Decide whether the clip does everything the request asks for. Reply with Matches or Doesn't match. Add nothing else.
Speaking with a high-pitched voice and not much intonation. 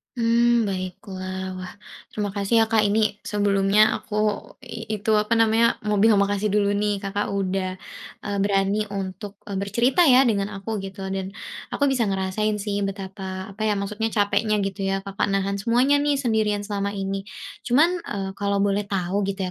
Matches